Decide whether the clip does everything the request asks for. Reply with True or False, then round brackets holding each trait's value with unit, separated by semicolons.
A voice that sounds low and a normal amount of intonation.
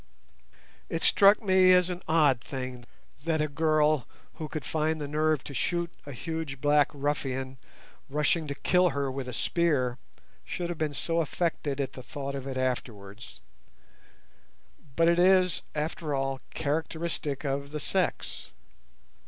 False (150 Hz; 3.5 semitones)